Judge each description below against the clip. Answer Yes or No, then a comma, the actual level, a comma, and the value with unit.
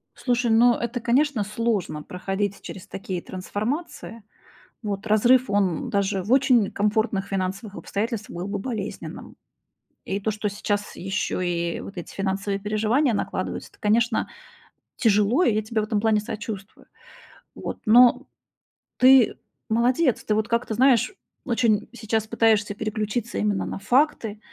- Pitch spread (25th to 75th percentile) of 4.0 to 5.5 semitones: No, average, 2.8 semitones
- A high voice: Yes, high, 215 Hz